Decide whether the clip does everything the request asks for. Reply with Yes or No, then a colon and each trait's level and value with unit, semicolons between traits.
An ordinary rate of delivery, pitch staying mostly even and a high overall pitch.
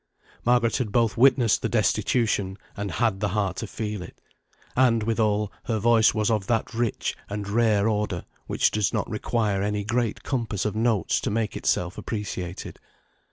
No: average, 165 wpm; narrow, 2.3 semitones; low, 110 Hz